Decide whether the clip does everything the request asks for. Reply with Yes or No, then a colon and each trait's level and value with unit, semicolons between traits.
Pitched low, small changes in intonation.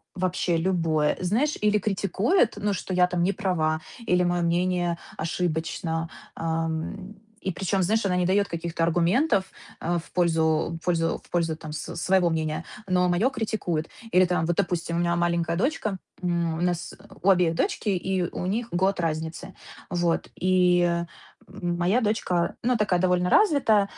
No: medium, 175 Hz; narrow, 2.3 semitones